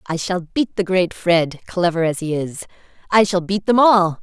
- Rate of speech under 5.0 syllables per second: Yes, 4.6 syllables/s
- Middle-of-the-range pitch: Yes, medium, 180 Hz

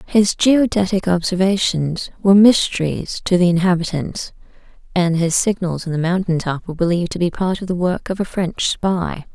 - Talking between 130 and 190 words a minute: Yes, average, 175 wpm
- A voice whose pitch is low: No, medium, 180 Hz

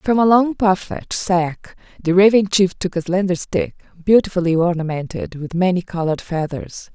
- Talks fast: No, average, 155 wpm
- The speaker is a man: No, female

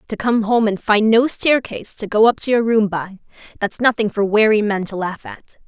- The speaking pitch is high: Yes, high, 215 Hz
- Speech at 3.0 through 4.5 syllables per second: No, 5.1 syllables/s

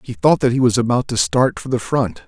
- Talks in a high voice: No, low, 120 Hz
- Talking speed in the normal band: No, fast, 290 wpm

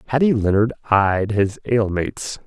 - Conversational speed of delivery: No, slow, 120 wpm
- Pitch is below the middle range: Yes, low, 110 Hz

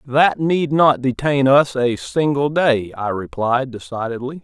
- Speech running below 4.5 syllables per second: Yes, 4.0 syllables/s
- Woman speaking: No, male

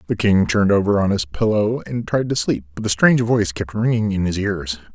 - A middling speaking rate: No, fast, 245 wpm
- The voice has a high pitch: No, low, 100 Hz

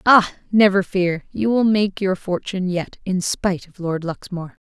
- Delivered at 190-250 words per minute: No, average, 180 wpm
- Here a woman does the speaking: Yes, female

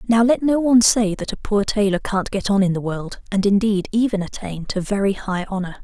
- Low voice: No, high, 205 Hz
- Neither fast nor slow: No, fast, 235 wpm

